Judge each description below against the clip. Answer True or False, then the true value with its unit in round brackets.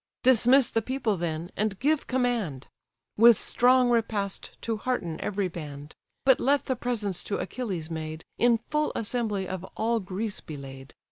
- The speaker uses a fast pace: False (155 wpm)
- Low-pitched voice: False (215 Hz)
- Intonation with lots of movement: True (6.1 semitones)